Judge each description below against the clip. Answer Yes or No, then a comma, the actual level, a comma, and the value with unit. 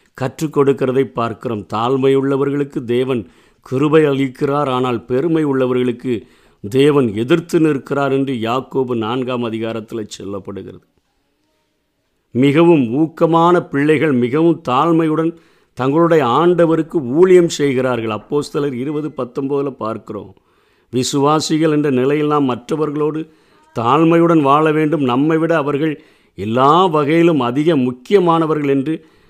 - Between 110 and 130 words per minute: No, average, 95 wpm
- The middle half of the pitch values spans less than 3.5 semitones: No, average, 4.0 semitones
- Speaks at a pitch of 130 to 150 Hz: Yes, medium, 140 Hz